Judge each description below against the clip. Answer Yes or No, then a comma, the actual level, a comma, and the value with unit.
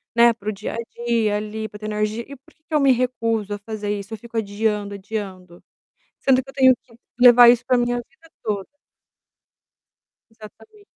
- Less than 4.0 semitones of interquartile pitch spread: Yes, average, 2.9 semitones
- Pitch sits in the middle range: No, high, 225 Hz